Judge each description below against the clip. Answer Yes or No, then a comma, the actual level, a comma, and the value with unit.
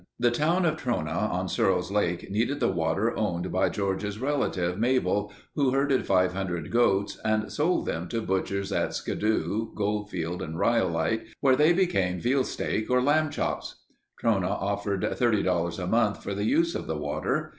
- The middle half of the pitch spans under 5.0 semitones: No, wide, 5.4 semitones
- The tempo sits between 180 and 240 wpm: No, average, 165 wpm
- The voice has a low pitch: Yes, low, 105 Hz